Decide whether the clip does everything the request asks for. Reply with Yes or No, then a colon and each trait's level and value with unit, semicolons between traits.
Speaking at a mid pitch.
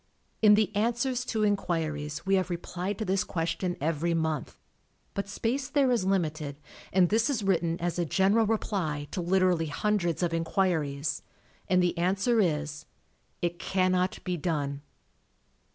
Yes: medium, 180 Hz